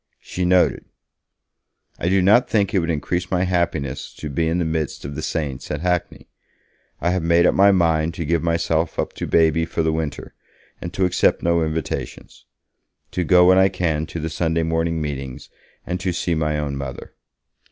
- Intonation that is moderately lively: No, narrow, 2.2 semitones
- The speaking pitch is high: No, very low, 85 Hz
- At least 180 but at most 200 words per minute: Yes, average, 195 wpm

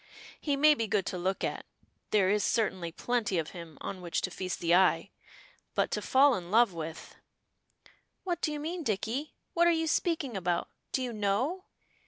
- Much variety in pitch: Yes, wide, 8.1 semitones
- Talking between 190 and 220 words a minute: Yes, average, 195 wpm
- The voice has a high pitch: Yes, high, 210 Hz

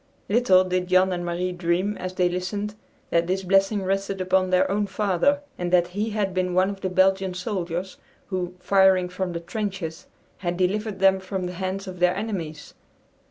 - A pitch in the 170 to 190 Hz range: Yes, medium, 185 Hz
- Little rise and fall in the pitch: Yes, narrow, 1.4 semitones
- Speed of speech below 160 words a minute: No, average, 185 wpm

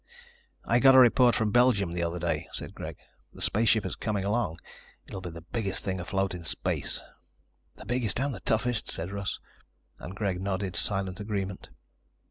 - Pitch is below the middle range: Yes, low, 100 Hz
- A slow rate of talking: No, average, 175 wpm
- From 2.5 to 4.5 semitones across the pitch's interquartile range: Yes, average, 3.5 semitones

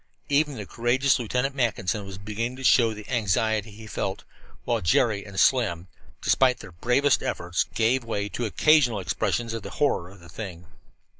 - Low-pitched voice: Yes, low, 110 Hz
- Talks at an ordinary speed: Yes, average, 170 wpm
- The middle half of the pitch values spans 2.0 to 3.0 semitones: No, average, 4.0 semitones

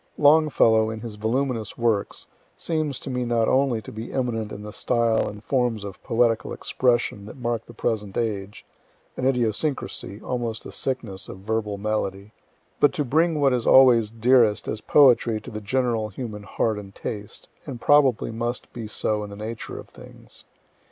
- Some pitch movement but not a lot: Yes, average, 3.0 semitones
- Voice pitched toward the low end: Yes, low, 115 Hz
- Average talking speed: Yes, average, 170 wpm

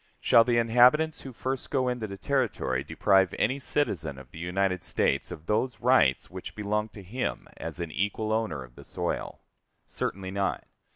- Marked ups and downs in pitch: Yes, wide, 5.7 semitones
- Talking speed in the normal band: Yes, average, 175 wpm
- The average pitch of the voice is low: Yes, low, 105 Hz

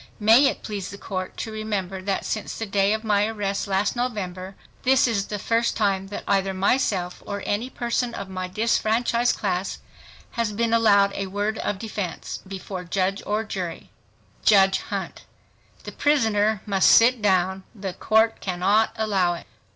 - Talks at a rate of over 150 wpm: Yes, average, 160 wpm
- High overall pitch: Yes, high, 205 Hz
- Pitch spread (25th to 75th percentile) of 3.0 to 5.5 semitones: No, narrow, 2.5 semitones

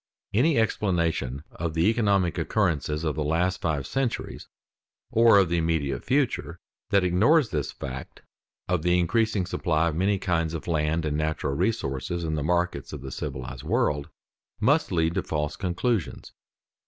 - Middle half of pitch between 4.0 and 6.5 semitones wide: Yes, average, 4.5 semitones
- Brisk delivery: No, average, 155 wpm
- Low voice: Yes, very low, 85 Hz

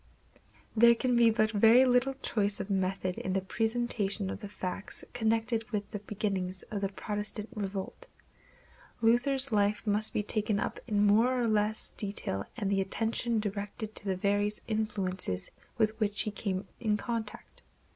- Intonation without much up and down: Yes, narrow, 2.1 semitones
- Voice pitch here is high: Yes, high, 210 Hz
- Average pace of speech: Yes, average, 160 wpm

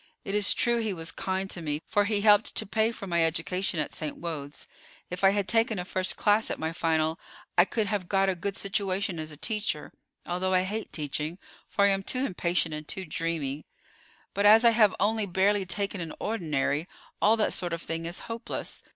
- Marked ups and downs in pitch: No, average, 3.8 semitones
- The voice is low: No, high, 190 Hz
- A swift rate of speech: Yes, fast, 210 wpm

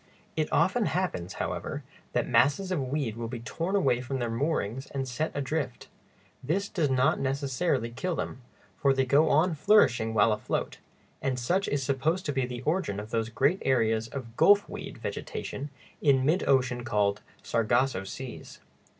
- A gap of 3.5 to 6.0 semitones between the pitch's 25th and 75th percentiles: Yes, average, 4.3 semitones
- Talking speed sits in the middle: Yes, average, 165 wpm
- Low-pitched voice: Yes, low, 130 Hz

